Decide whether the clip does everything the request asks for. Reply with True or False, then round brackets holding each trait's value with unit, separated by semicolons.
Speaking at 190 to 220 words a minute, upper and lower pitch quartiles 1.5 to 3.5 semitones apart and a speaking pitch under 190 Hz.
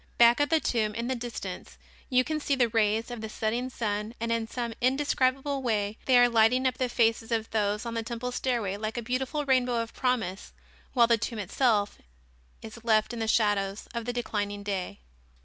False (200 wpm; 2.5 semitones; 230 Hz)